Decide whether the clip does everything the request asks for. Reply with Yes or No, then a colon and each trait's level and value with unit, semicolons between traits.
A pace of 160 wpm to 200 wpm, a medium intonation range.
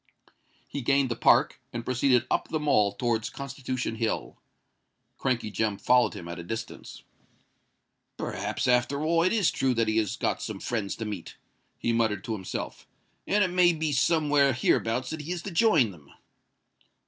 Yes: average, 170 wpm; average, 4.9 semitones